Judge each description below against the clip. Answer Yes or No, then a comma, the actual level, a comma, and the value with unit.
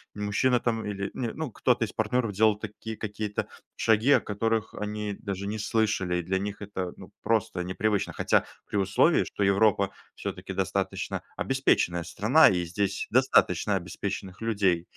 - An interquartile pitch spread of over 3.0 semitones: No, narrow, 2.4 semitones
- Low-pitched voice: Yes, low, 105 Hz